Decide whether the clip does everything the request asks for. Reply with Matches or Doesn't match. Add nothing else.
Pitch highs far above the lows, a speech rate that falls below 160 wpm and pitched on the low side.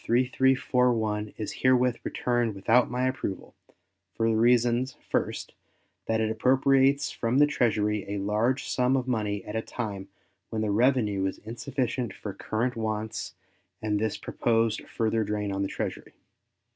Doesn't match